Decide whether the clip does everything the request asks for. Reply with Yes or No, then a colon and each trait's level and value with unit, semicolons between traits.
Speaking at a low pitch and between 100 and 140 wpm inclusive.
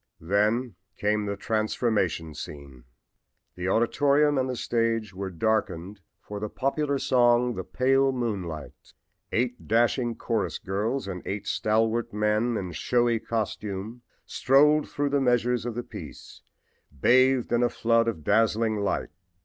Yes: low, 115 Hz; slow, 135 wpm